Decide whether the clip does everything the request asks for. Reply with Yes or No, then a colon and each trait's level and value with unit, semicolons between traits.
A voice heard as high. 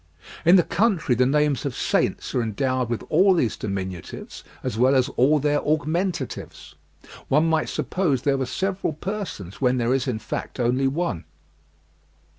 No: low, 135 Hz